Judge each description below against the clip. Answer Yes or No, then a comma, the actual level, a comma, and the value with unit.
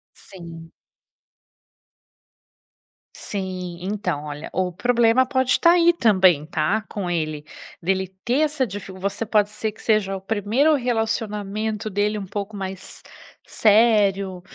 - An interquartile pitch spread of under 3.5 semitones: Yes, average, 3.1 semitones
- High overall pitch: Yes, high, 205 Hz